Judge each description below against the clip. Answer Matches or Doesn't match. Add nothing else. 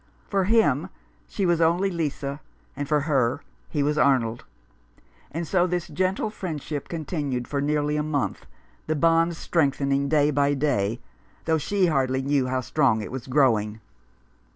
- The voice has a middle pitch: Matches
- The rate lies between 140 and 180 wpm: Matches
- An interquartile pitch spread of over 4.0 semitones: Doesn't match